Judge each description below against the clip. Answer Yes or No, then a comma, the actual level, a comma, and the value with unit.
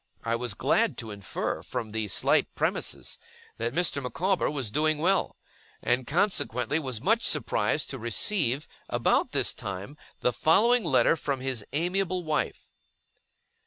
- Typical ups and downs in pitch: No, wide, 6.6 semitones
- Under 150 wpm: Yes, average, 140 wpm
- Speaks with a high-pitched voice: No, medium, 140 Hz